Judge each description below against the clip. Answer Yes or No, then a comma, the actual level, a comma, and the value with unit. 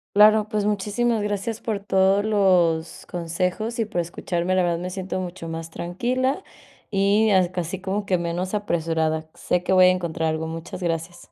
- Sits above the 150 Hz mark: Yes, medium, 185 Hz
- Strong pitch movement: No, average, 3.3 semitones